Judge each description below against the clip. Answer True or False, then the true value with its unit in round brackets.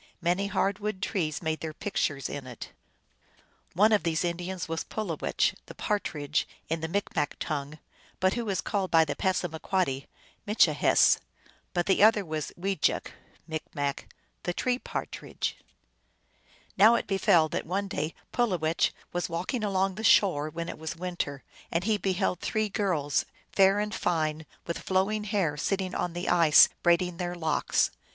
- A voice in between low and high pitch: True (180 Hz)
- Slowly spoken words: False (155 wpm)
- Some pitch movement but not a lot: True (3.9 semitones)